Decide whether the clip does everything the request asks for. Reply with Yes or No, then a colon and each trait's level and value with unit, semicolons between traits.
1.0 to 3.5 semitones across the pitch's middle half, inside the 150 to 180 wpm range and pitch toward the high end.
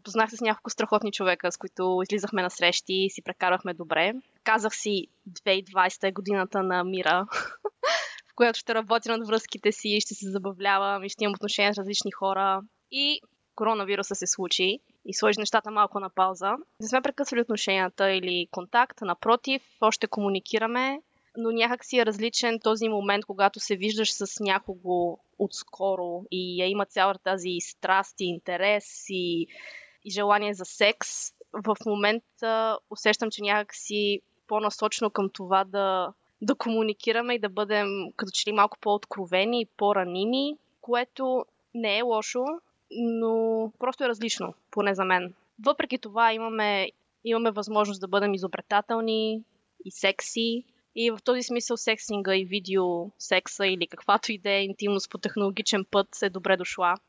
Yes: average, 2.8 semitones; average, 155 wpm; high, 205 Hz